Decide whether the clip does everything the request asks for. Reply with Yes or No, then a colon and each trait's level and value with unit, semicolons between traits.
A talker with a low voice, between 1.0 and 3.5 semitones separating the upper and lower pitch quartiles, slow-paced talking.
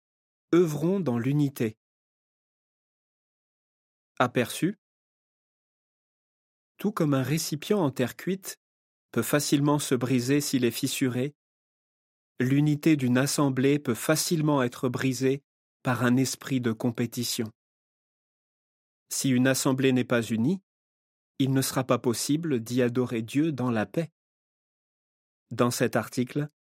Yes: low, 130 Hz; average, 3.0 semitones; slow, 110 wpm